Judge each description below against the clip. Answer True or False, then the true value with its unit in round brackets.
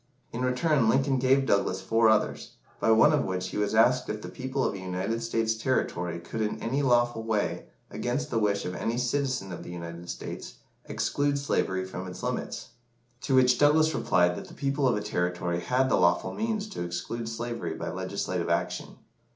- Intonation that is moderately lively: False (5.8 semitones)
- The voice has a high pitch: False (115 Hz)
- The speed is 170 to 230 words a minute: True (190 wpm)